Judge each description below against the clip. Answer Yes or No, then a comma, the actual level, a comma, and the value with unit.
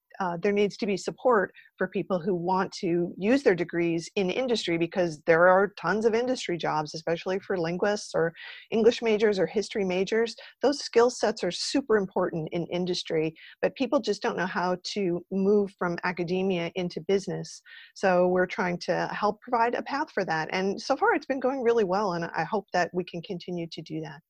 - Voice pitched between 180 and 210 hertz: Yes, high, 190 Hz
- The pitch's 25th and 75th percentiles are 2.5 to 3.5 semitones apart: No, average, 4.0 semitones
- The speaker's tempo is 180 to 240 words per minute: Yes, average, 200 wpm